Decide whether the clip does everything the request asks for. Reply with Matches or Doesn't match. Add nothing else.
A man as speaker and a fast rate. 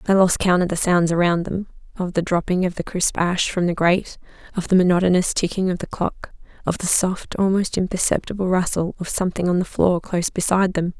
Doesn't match